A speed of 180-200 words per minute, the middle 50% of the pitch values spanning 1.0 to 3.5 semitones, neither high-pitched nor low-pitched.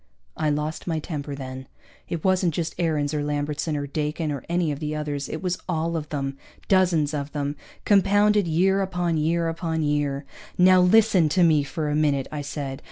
Yes: average, 190 wpm; average, 3.0 semitones; medium, 155 Hz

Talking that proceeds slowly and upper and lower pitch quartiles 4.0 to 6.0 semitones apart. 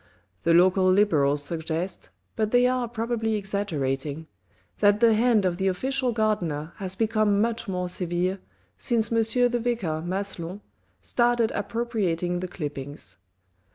Yes: slow, 130 wpm; average, 4.6 semitones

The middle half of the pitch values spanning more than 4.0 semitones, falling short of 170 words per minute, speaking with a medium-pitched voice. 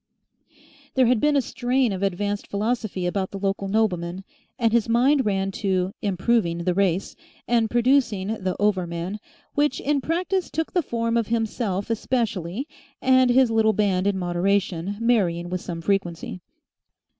No: average, 4.4 semitones; average, 155 wpm; high, 205 Hz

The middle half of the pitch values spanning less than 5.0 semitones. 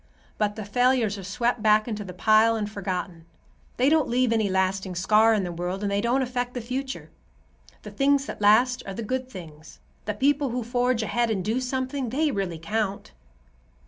Yes: average, 4.2 semitones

